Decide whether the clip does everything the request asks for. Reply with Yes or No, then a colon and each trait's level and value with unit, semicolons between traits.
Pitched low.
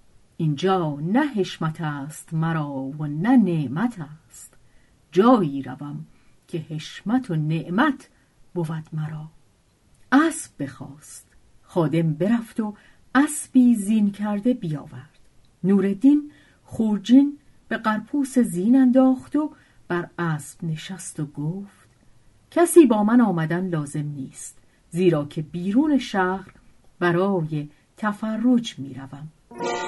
No: medium, 170 Hz